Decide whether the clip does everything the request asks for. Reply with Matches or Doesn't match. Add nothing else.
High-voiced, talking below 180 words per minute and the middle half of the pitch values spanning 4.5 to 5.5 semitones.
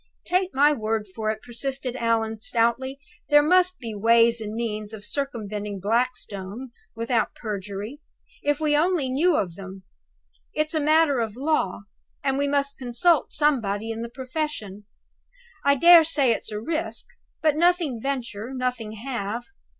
Matches